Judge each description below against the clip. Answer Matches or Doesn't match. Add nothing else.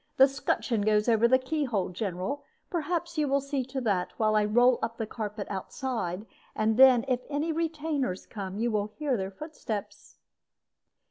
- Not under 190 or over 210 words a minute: Doesn't match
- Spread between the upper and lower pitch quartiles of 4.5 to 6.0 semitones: Matches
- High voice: Matches